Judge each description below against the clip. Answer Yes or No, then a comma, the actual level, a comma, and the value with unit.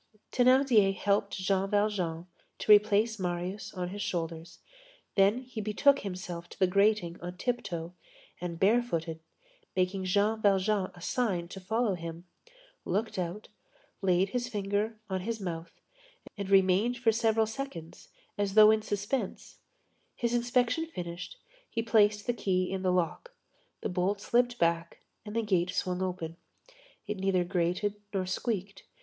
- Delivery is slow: No, average, 145 wpm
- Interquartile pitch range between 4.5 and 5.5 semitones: No, average, 3.3 semitones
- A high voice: Yes, high, 200 Hz